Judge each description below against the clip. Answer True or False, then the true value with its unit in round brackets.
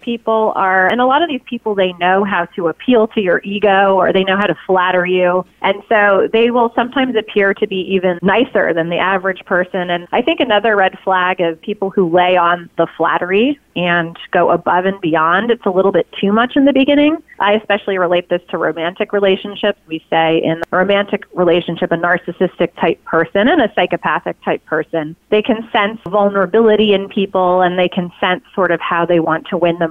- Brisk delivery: True (210 wpm)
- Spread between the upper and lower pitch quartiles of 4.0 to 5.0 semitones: False (3.0 semitones)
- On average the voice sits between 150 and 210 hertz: True (190 Hz)